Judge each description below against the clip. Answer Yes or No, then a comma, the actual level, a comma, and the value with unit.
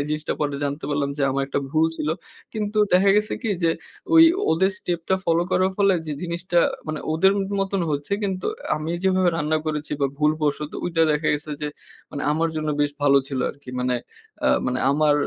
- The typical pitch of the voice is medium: Yes, medium, 155 Hz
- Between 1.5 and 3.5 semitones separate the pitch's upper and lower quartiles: No, average, 3.9 semitones